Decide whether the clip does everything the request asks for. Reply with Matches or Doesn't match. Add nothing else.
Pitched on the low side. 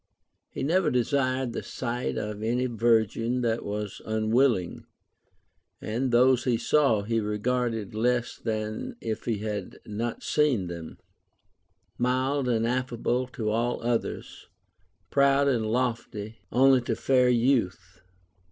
Matches